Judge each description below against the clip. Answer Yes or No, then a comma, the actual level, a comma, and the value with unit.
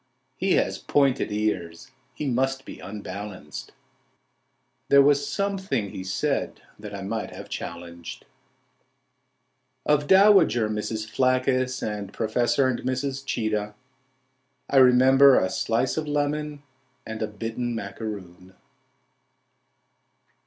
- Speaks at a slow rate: Yes, slow, 110 wpm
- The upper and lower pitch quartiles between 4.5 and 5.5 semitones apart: Yes, average, 4.8 semitones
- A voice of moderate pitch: No, low, 120 Hz